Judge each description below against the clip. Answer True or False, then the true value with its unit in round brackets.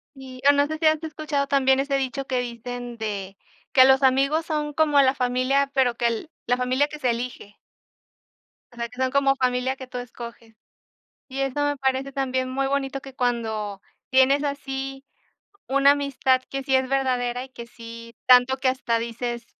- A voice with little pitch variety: True (2.0 semitones)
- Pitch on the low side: False (260 Hz)